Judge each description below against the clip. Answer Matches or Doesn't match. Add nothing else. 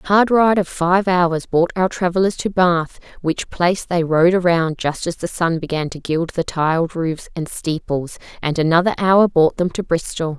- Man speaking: Doesn't match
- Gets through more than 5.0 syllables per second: Doesn't match